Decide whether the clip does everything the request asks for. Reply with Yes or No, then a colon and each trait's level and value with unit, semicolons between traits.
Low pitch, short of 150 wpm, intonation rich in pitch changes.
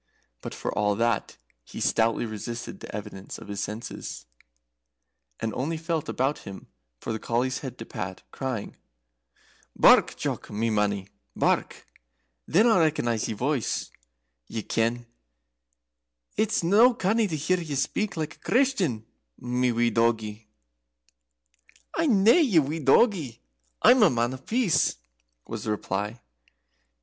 Yes: low, 125 Hz; slow, 135 wpm; wide, 7.3 semitones